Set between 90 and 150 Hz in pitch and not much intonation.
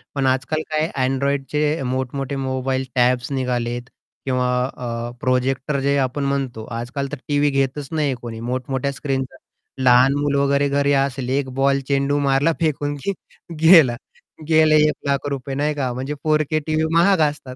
Yes: low, 135 Hz; narrow, 2.1 semitones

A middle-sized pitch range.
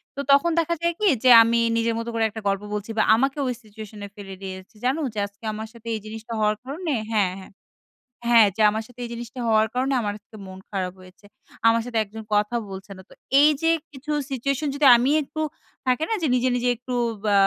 Yes: average, 3.7 semitones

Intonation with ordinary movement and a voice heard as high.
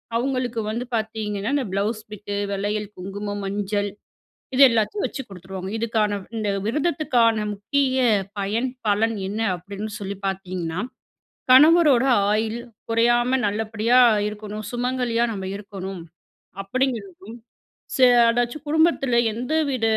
Yes: average, 3.5 semitones; high, 220 Hz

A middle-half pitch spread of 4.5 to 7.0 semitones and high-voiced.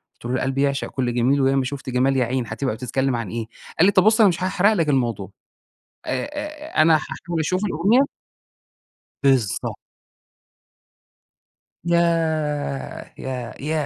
No: average, 5.0 semitones; medium, 140 Hz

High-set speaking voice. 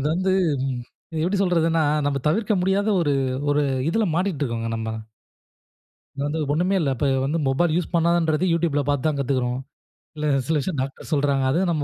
No: medium, 155 Hz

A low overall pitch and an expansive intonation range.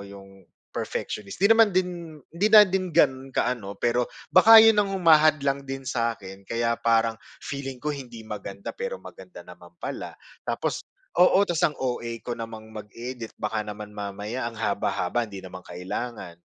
Yes: low, 120 Hz; wide, 6.9 semitones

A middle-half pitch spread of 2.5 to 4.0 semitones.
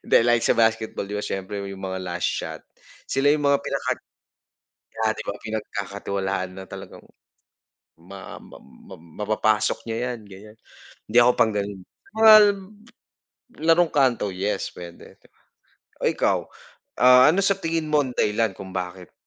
No: average, 4.4 semitones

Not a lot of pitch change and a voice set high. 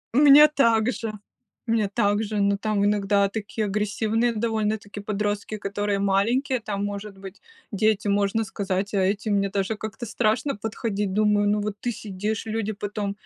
Yes: narrow, 1.6 semitones; high, 210 Hz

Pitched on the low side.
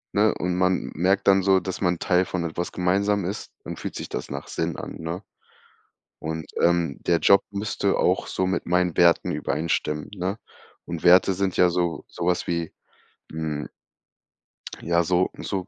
Yes: very low, 90 Hz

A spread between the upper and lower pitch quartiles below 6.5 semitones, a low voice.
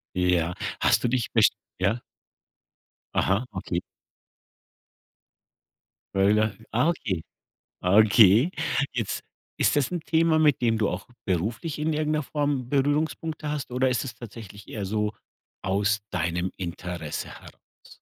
No: wide, 7.0 semitones; low, 110 Hz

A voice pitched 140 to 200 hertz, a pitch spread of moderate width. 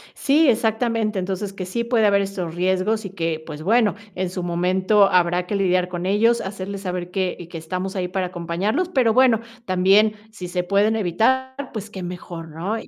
Yes: high, 190 Hz; average, 3.4 semitones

